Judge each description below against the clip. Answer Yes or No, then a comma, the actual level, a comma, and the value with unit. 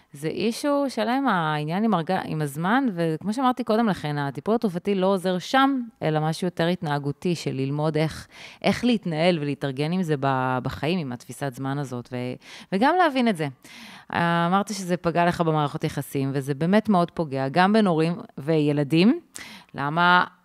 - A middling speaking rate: No, fast, 155 wpm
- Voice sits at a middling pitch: Yes, medium, 170 Hz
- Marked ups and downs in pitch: Yes, wide, 6.2 semitones